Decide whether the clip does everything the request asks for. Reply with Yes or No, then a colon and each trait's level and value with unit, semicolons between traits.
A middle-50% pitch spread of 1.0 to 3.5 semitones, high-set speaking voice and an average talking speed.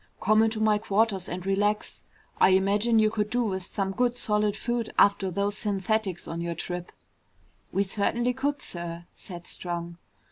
Yes: average, 3.0 semitones; high, 200 Hz; average, 165 wpm